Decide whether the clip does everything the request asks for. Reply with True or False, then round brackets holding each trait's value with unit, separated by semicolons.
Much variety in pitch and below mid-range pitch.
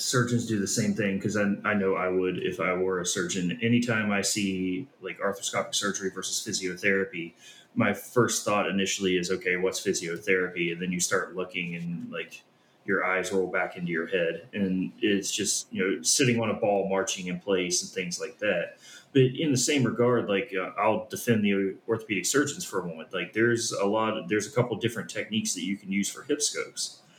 False (3.2 semitones; 95 Hz)